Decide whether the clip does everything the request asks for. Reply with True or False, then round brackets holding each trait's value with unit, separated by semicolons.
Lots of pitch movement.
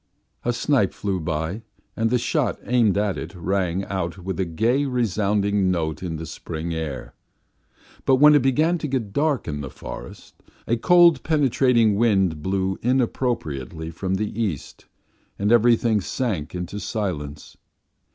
True (6.1 semitones)